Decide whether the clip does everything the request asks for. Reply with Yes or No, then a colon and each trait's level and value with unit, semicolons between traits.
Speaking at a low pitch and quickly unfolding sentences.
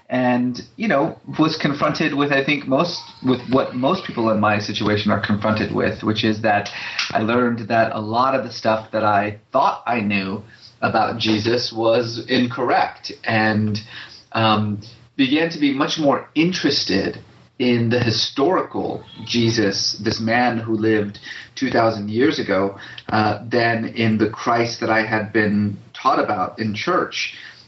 No: low, 115 Hz; average, 155 wpm